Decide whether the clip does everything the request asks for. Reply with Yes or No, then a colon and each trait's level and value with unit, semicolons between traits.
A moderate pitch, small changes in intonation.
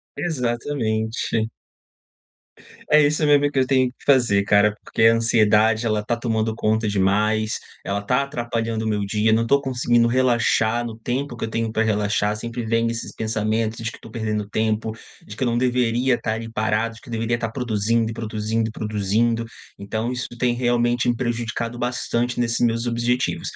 No: low, 115 Hz; narrow, 1.7 semitones